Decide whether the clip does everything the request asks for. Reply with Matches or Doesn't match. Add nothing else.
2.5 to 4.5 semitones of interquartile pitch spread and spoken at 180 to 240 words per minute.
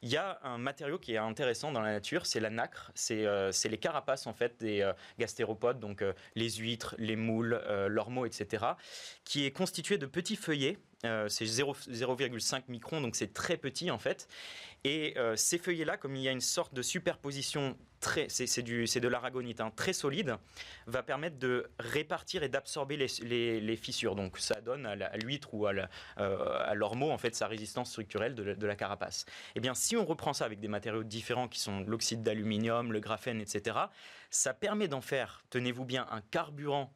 Matches